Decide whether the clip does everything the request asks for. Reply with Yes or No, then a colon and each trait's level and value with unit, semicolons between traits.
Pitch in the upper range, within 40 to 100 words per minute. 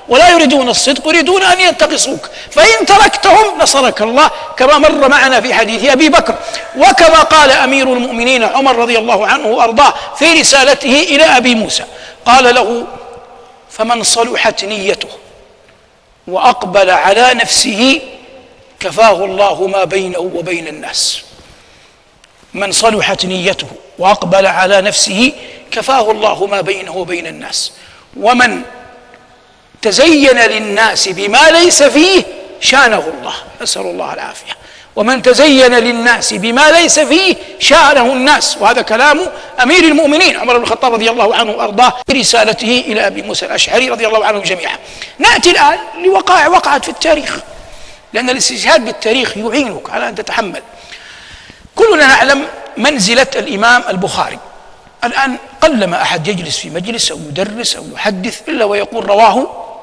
No: very high, 250 Hz; average, 125 wpm